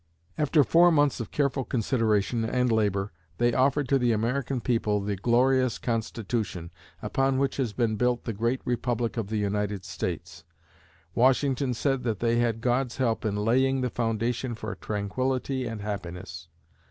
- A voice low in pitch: Yes, low, 120 Hz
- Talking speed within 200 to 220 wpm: No, average, 155 wpm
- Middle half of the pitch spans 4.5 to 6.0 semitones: No, average, 3.6 semitones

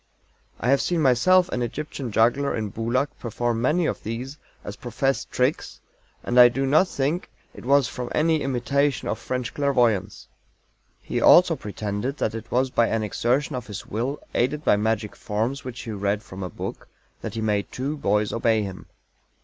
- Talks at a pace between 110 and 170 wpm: No, average, 180 wpm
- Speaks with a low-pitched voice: Yes, low, 120 Hz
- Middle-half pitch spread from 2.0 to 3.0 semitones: No, average, 4.0 semitones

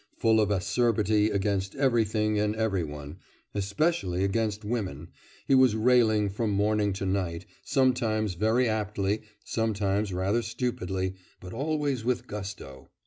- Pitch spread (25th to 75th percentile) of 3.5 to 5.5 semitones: No, average, 2.8 semitones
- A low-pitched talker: Yes, low, 105 Hz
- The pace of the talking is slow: Yes, slow, 130 wpm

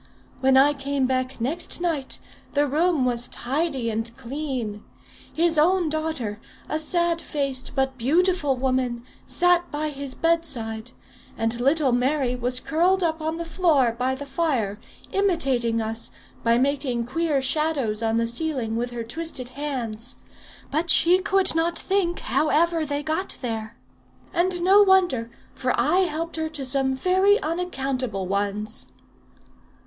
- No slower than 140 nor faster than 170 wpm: Yes, average, 145 wpm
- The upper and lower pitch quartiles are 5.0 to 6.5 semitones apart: Yes, average, 5.3 semitones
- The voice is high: Yes, very high, 280 Hz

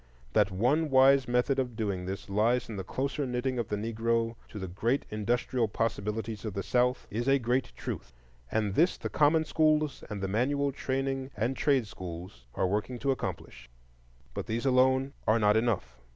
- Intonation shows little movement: No, average, 4.2 semitones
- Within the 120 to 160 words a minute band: No, average, 180 wpm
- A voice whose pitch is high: No, low, 120 Hz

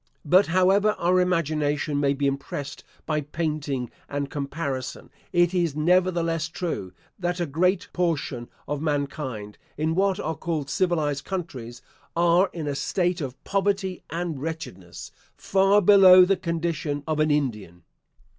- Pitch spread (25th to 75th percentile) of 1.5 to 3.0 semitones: No, average, 4.1 semitones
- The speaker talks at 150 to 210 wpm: No, slow, 135 wpm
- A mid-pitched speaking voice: Yes, medium, 160 Hz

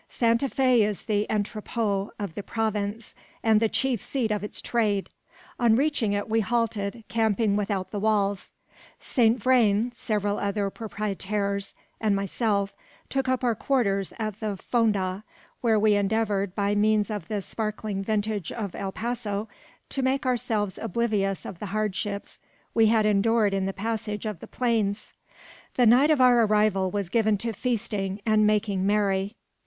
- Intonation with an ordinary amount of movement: No, narrow, 2.2 semitones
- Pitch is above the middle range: Yes, high, 215 Hz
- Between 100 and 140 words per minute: No, average, 160 wpm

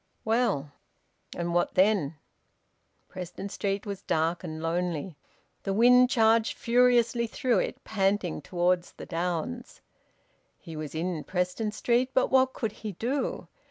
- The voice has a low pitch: No, high, 195 Hz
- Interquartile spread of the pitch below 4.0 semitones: No, average, 5.3 semitones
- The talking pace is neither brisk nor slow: No, slow, 130 wpm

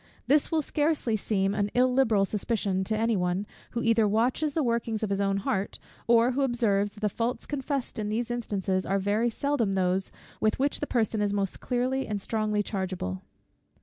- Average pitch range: Yes, average, 3.7 semitones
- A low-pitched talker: No, high, 220 Hz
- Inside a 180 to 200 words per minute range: Yes, average, 185 wpm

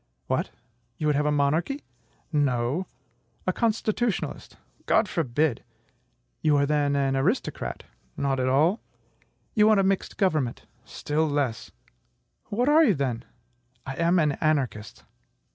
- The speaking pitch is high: No, medium, 150 Hz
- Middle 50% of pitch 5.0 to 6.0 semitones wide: Yes, wide, 5.6 semitones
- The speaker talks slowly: Yes, slow, 130 wpm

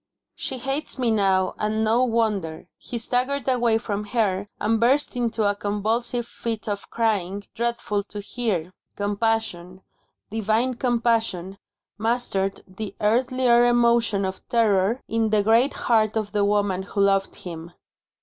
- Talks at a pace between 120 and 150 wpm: Yes, average, 140 wpm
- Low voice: No, high, 220 Hz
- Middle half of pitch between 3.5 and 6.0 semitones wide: No, average, 2.9 semitones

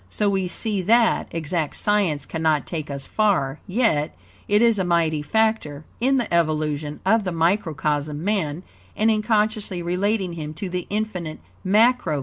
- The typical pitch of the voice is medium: Yes, medium, 180 Hz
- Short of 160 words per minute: No, average, 170 wpm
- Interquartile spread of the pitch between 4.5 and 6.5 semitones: Yes, wide, 5.5 semitones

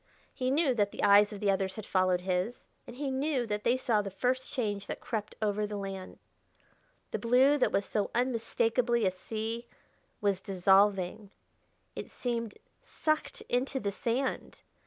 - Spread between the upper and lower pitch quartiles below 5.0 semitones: Yes, average, 3.8 semitones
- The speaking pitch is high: Yes, high, 215 Hz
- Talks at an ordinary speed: Yes, average, 165 wpm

